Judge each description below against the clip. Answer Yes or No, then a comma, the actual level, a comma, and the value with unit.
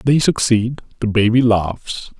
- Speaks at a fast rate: No, slow, 135 wpm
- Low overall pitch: Yes, low, 115 Hz